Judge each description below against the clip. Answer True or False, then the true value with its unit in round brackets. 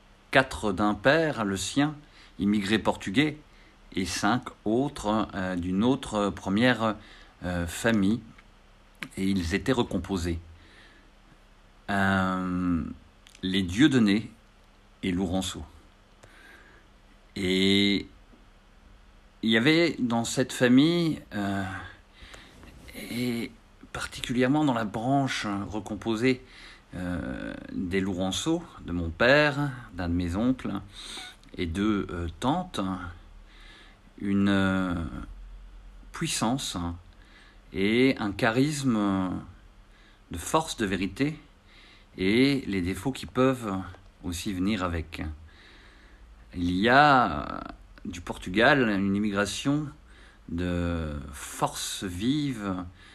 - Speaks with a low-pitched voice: True (100 Hz)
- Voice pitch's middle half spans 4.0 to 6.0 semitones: True (4.3 semitones)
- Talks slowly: True (95 wpm)